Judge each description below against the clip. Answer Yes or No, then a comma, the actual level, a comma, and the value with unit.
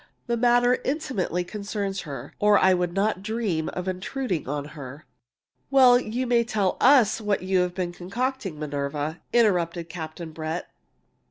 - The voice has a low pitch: No, medium, 185 Hz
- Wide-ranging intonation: Yes, wide, 6.2 semitones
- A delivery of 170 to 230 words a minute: No, average, 155 wpm